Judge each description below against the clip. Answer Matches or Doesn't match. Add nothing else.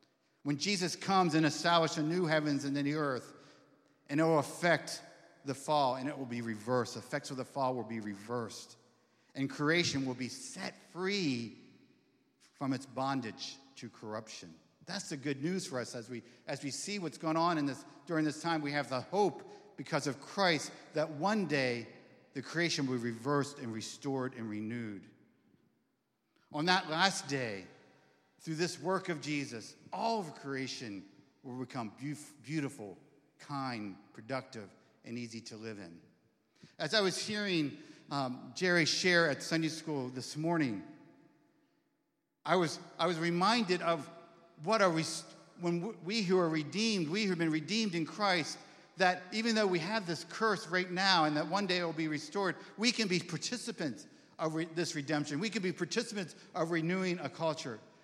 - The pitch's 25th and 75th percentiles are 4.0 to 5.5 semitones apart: Matches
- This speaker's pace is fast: Doesn't match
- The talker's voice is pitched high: Doesn't match